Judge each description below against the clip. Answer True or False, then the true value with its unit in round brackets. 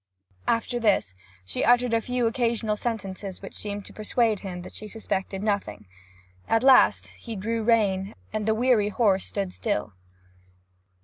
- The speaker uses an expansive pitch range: False (2.9 semitones)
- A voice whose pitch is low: False (215 Hz)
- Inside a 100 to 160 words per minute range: True (150 wpm)